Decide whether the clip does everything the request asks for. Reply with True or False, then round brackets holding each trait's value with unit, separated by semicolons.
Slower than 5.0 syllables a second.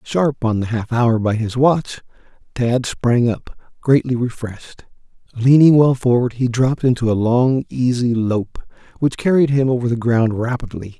True (4.6 syllables/s)